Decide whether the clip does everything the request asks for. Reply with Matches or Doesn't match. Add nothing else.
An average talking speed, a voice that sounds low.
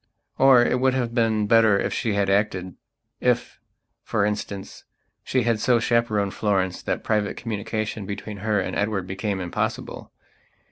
Matches